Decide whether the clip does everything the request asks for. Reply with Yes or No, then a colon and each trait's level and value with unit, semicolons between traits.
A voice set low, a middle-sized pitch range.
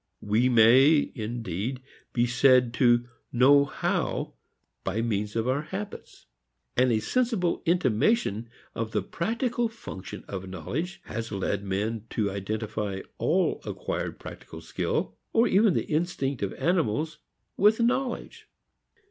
No: low, 125 Hz; wide, 8.2 semitones